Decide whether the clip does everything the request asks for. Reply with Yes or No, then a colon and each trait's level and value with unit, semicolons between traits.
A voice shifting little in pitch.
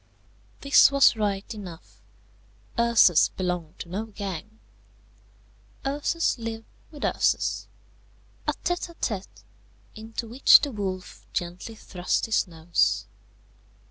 No: average, 4.4 semitones